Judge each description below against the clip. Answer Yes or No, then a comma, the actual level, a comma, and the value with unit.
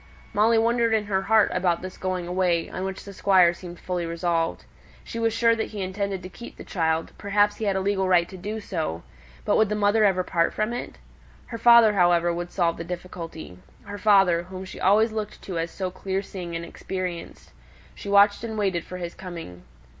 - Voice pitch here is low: No, high, 190 Hz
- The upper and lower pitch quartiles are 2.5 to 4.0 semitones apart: Yes, average, 3.1 semitones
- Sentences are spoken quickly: Yes, fast, 210 wpm